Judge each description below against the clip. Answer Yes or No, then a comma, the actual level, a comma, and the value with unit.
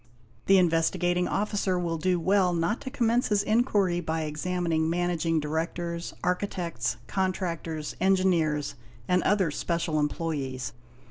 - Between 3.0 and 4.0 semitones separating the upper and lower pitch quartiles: No, narrow, 2.6 semitones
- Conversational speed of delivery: No, slow, 120 wpm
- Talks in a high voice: No, medium, 175 Hz